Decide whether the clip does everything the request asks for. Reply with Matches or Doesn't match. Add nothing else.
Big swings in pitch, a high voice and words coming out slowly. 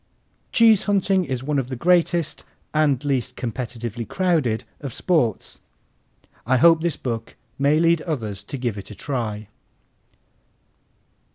Doesn't match